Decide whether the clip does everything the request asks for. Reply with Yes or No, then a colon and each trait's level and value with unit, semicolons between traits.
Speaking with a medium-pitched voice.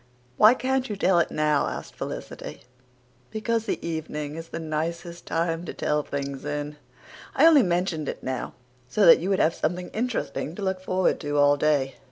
Yes: medium, 165 Hz